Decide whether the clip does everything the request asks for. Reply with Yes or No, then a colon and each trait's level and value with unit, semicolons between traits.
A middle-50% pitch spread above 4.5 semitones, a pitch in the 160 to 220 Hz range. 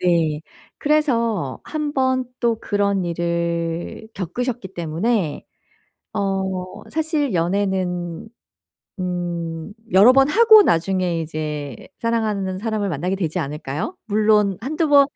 Yes: wide, 5.5 semitones; high, 190 Hz